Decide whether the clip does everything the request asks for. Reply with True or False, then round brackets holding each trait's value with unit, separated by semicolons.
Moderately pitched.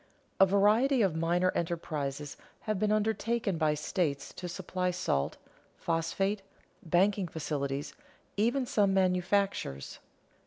True (180 Hz)